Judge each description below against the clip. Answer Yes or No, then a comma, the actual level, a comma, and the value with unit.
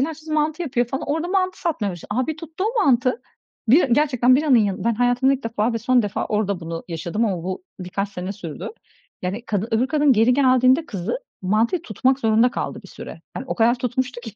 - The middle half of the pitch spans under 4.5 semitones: No, average, 5.0 semitones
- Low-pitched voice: No, high, 245 Hz